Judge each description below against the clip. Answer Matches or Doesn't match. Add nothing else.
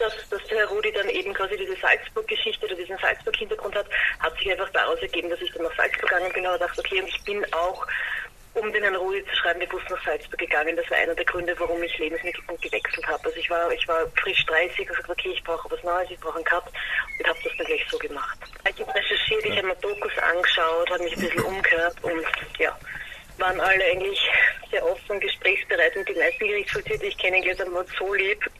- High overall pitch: Matches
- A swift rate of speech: Matches